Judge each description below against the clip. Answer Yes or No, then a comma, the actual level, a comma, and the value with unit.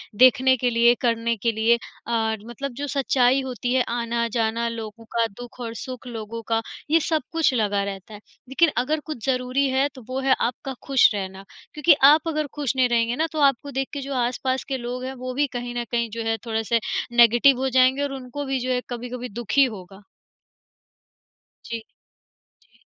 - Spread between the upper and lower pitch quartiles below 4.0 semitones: Yes, narrow, 2.6 semitones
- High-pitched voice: Yes, high, 245 Hz